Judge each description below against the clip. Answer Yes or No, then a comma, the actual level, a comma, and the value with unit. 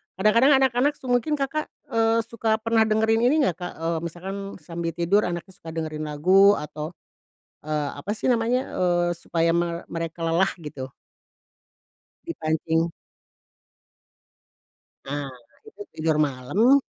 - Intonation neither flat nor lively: No, wide, 6.2 semitones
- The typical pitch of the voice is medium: Yes, medium, 175 Hz